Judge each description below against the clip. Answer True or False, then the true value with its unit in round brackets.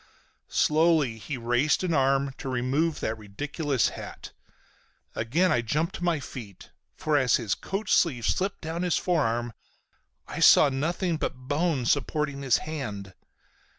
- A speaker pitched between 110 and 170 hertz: True (140 Hz)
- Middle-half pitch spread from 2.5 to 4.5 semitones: False (4.9 semitones)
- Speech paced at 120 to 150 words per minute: True (145 wpm)